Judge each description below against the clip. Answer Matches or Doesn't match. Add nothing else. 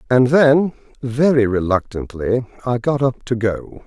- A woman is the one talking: Doesn't match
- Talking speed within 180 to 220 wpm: Doesn't match